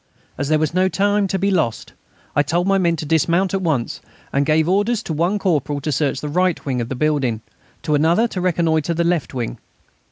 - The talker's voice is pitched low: No, medium, 160 Hz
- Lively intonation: No, average, 4.2 semitones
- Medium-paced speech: No, fast, 220 wpm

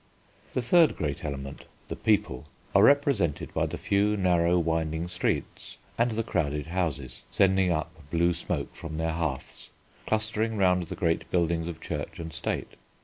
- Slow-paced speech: No, average, 155 wpm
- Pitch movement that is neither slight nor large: Yes, average, 4.1 semitones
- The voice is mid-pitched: No, very low, 85 Hz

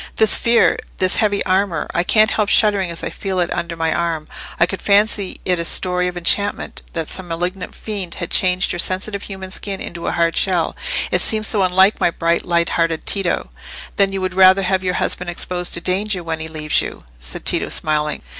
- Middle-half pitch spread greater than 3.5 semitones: No, narrow, 2.5 semitones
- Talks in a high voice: No, medium, 180 Hz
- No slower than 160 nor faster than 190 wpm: No, average, 200 wpm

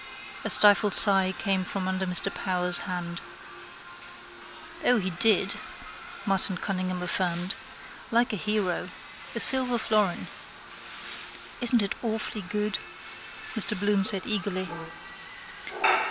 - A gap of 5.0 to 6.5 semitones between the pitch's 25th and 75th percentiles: No, narrow, 2.5 semitones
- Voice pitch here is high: Yes, high, 195 Hz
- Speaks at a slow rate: Yes, slow, 110 wpm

